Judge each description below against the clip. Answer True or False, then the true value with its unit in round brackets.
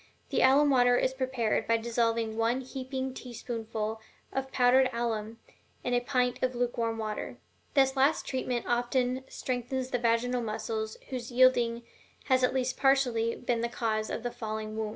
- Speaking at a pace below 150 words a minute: False (160 wpm)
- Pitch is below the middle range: False (245 Hz)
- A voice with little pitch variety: True (2.2 semitones)